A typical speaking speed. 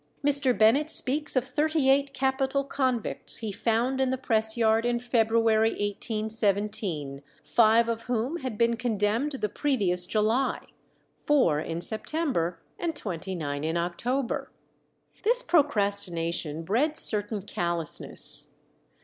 No: slow, 125 wpm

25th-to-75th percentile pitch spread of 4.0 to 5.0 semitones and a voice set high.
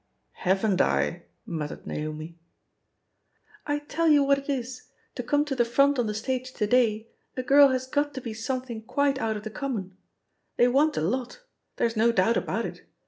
Yes: average, 4.3 semitones; very high, 250 Hz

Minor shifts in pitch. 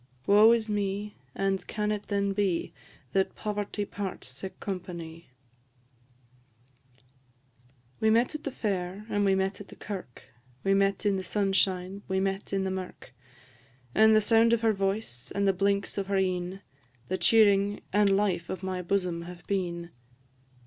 Yes: narrow, 1.8 semitones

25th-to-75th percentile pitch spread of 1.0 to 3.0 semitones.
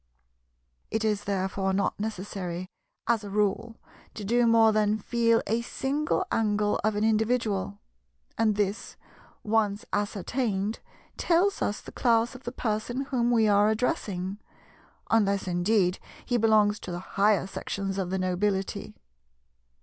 Yes: narrow, 2.5 semitones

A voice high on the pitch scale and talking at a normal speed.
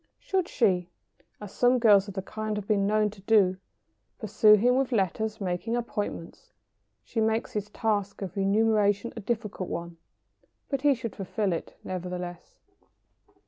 Yes: high, 210 Hz; average, 150 wpm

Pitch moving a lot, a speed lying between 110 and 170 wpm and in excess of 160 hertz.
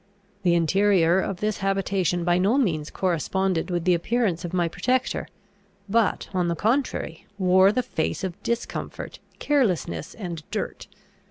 No: average, 3.2 semitones; average, 145 wpm; medium, 185 Hz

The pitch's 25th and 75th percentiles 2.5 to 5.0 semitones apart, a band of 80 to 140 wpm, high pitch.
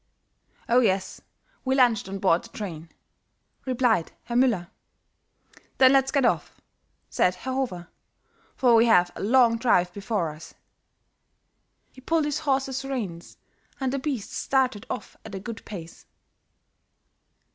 No: wide, 5.5 semitones; slow, 135 wpm; high, 230 Hz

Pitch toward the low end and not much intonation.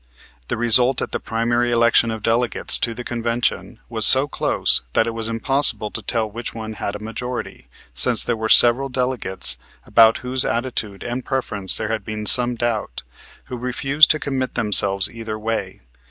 Yes: low, 115 Hz; narrow, 2.1 semitones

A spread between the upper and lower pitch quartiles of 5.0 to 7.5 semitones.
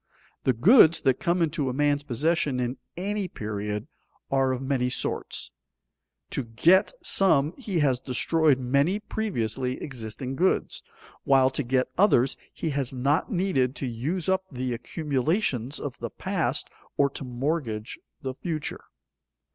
No: average, 4.6 semitones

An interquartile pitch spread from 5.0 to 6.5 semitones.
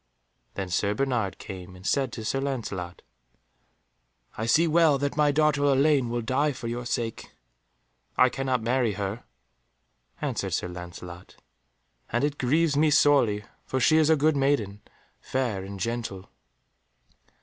Yes: wide, 5.6 semitones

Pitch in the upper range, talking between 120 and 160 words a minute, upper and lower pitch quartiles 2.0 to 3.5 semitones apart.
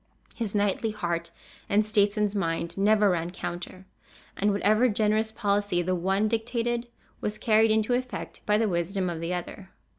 Yes: high, 205 Hz; average, 155 wpm; average, 2.9 semitones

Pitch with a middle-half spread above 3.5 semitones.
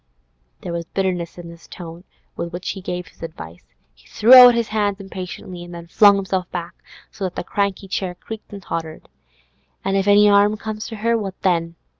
No: average, 3.0 semitones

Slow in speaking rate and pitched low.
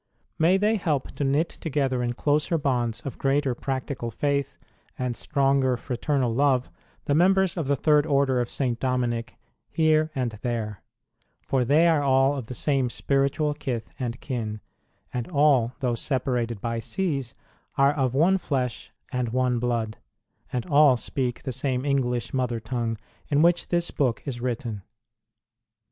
No: average, 155 wpm; low, 130 Hz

